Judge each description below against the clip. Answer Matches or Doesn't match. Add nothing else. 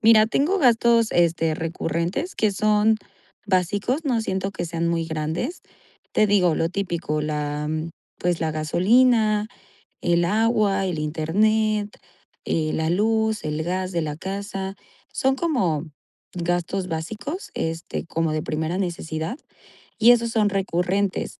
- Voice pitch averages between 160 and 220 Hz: Matches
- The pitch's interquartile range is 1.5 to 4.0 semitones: Doesn't match